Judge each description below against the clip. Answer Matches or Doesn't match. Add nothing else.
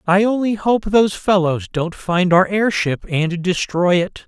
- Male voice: Matches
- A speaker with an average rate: Matches